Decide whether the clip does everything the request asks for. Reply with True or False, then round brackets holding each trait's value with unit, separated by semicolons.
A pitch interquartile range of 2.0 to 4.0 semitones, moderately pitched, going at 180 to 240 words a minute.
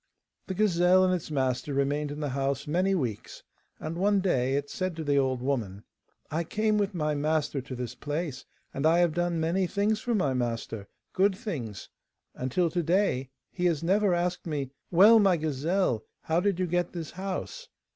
False (5.0 semitones; 165 Hz; 190 wpm)